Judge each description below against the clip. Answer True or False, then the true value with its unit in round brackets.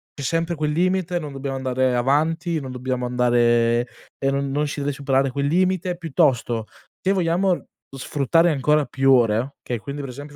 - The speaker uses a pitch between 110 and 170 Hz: True (140 Hz)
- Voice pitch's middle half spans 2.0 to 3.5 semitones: False (4.4 semitones)